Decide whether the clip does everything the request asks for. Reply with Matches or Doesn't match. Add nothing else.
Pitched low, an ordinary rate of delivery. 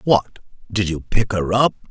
Matches